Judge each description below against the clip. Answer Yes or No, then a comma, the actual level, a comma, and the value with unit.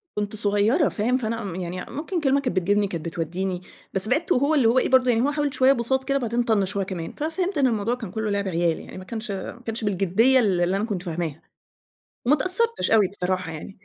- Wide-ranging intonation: Yes, wide, 5.7 semitones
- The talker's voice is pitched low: No, high, 220 Hz